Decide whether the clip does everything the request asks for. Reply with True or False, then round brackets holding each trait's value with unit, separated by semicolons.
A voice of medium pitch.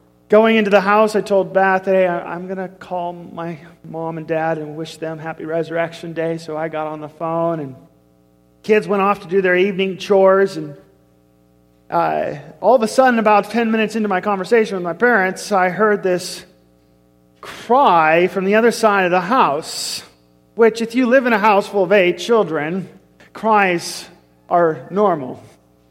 True (180 Hz)